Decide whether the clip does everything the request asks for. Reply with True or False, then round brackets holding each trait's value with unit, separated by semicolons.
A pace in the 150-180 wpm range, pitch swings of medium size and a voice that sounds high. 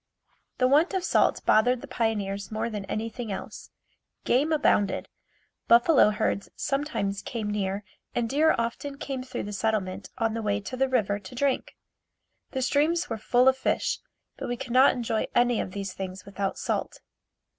True (170 wpm; 4.3 semitones; 230 Hz)